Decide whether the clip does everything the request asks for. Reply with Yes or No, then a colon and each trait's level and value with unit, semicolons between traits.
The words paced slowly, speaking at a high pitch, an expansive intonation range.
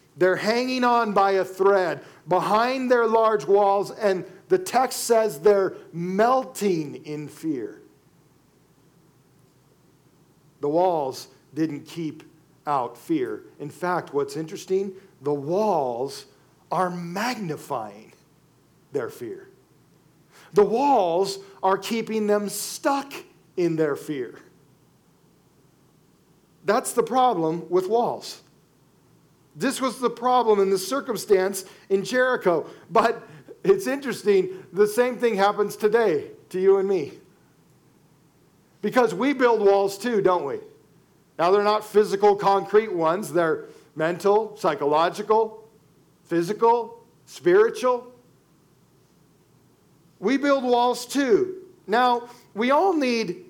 Yes: slow, 105 wpm; high, 205 Hz; wide, 5.8 semitones